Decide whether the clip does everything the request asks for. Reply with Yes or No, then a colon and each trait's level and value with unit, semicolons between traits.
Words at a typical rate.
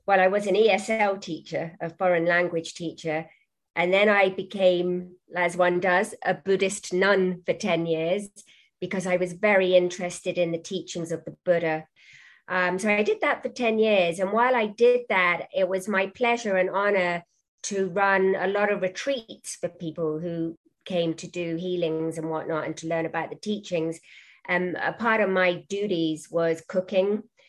Yes: average, 180 wpm